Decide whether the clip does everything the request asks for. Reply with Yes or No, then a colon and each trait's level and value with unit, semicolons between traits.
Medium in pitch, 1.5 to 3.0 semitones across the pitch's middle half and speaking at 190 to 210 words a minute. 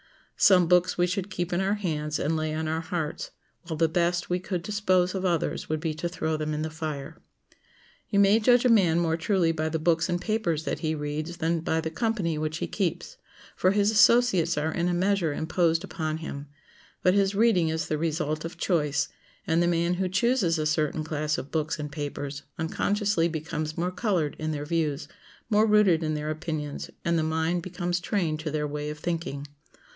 Yes: medium, 165 Hz; average, 2.7 semitones; fast, 205 wpm